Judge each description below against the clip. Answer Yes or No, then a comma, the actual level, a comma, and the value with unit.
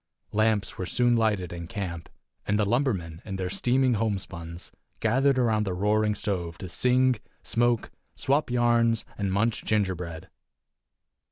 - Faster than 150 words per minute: No, average, 140 wpm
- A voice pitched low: Yes, low, 105 Hz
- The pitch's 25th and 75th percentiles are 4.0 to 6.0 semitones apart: Yes, average, 4.3 semitones